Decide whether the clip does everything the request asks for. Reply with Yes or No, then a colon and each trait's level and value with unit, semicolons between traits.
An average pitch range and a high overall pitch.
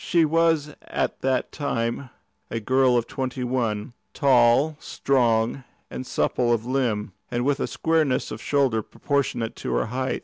No: average, 3.1 semitones; low, 130 Hz